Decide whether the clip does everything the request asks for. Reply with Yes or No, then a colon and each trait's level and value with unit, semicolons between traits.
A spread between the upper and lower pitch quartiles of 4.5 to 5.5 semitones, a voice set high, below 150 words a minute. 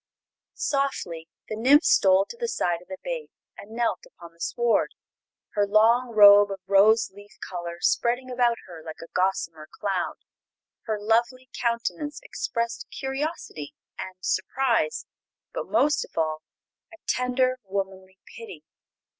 Yes: average, 5.1 semitones; high, 215 Hz; average, 140 wpm